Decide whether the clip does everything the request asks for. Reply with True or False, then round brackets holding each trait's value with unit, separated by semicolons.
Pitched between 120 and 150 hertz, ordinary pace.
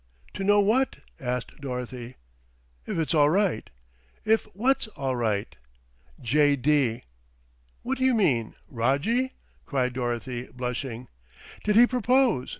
False (140 Hz; 125 wpm)